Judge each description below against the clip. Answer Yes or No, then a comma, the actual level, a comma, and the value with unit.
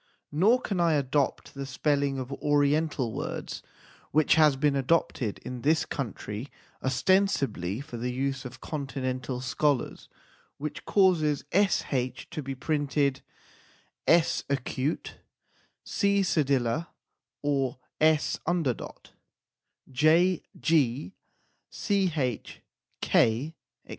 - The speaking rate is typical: No, slow, 95 wpm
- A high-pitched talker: No, medium, 140 Hz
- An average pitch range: Yes, average, 3.4 semitones